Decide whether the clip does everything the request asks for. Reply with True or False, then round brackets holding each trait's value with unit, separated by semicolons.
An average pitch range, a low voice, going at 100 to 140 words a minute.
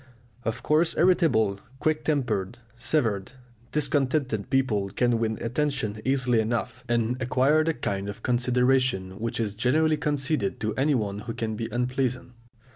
True (4.1 semitones; 125 Hz; 135 wpm)